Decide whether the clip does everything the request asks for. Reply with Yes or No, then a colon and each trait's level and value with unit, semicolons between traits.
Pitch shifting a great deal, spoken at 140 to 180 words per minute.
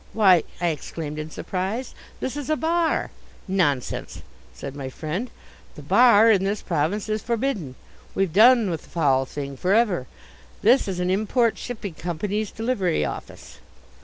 Yes: wide, 6.2 semitones; average, 155 wpm